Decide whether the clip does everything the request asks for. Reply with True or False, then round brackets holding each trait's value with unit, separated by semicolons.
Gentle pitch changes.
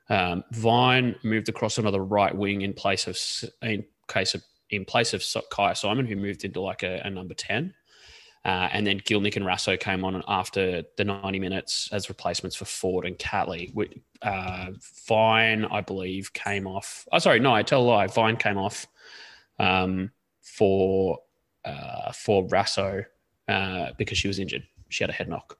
True (2.2 semitones)